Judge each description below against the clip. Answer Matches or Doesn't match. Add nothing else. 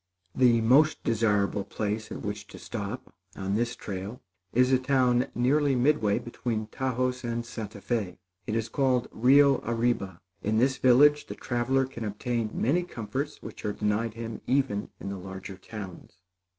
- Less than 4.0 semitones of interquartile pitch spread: Matches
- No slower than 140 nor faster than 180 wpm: Matches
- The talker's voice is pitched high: Doesn't match